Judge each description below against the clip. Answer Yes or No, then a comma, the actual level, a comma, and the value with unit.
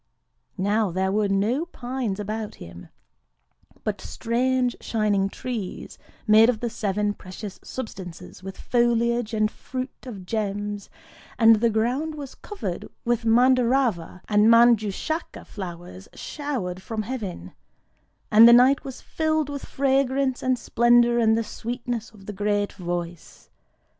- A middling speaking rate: No, slow, 125 wpm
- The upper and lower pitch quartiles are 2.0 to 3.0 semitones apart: No, average, 3.7 semitones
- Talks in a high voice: Yes, high, 225 Hz